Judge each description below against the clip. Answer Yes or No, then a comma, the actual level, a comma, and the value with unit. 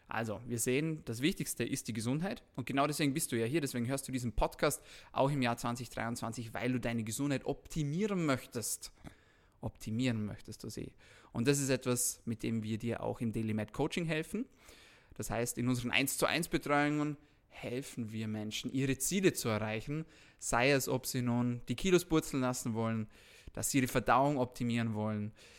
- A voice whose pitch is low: Yes, low, 125 Hz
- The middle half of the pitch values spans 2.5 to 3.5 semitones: No, average, 3.9 semitones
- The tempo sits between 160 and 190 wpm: Yes, average, 185 wpm